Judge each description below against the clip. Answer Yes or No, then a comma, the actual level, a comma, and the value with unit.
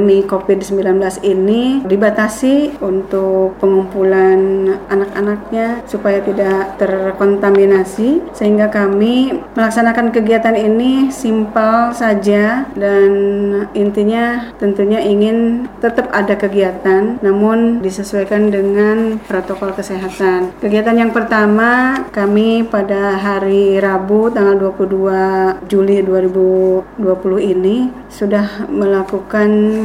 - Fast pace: No, slow, 85 wpm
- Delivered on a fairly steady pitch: Yes, narrow, 2.3 semitones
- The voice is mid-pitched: No, high, 200 Hz